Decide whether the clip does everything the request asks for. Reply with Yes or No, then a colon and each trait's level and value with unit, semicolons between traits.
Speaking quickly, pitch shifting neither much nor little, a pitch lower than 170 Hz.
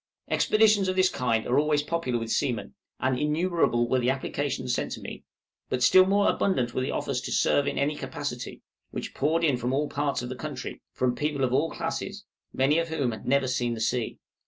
Yes: fast, 210 wpm; average, 4.4 semitones; medium, 140 Hz